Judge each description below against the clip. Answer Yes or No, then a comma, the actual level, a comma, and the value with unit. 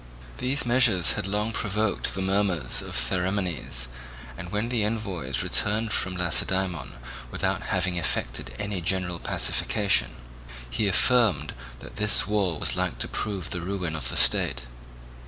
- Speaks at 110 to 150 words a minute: Yes, average, 140 wpm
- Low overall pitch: Yes, very low, 95 Hz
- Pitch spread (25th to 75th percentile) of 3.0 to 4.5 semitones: Yes, average, 3.4 semitones